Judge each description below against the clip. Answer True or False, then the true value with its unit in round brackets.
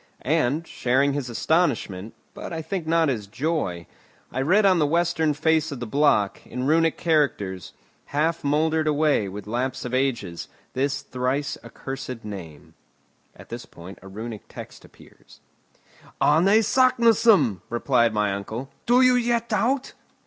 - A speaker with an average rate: True (145 wpm)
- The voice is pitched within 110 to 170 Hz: True (140 Hz)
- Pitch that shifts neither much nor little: False (6.1 semitones)